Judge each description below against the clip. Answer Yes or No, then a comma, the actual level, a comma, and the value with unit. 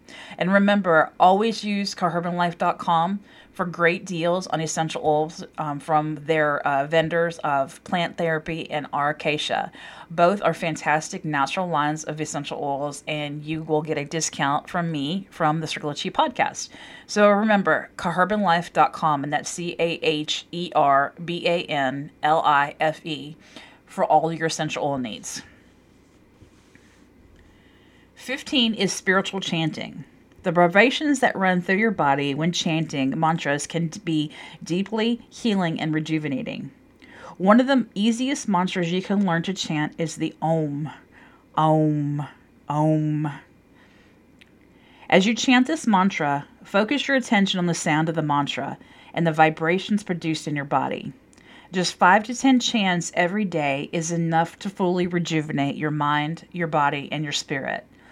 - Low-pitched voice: No, medium, 165 Hz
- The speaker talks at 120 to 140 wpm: Yes, slow, 135 wpm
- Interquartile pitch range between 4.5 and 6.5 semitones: No, average, 3.7 semitones